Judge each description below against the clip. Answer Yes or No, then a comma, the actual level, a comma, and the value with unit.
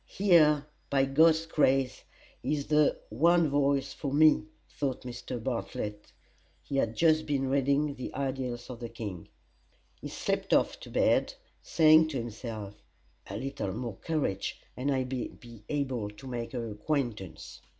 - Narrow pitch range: No, average, 4.0 semitones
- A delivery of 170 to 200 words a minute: No, average, 150 wpm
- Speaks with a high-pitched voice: No, low, 135 Hz